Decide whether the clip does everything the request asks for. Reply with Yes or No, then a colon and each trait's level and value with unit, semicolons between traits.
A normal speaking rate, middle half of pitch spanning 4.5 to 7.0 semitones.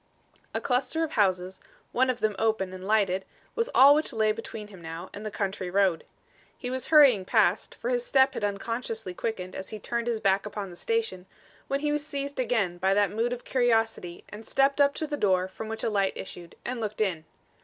No: fast, 215 wpm; average, 5.2 semitones